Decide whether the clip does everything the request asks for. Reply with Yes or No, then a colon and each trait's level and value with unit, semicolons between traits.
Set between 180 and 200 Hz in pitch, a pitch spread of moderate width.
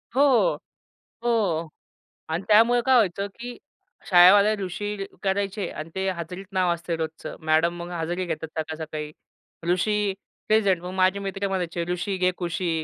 Yes: medium, 185 Hz; average, 3.1 semitones